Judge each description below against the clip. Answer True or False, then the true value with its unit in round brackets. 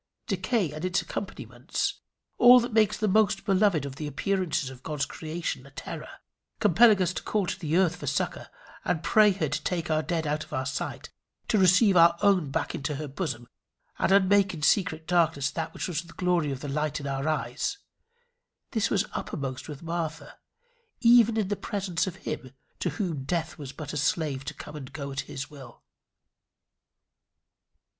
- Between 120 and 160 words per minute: False (190 wpm)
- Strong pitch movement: False (4.8 semitones)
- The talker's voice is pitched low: False (165 Hz)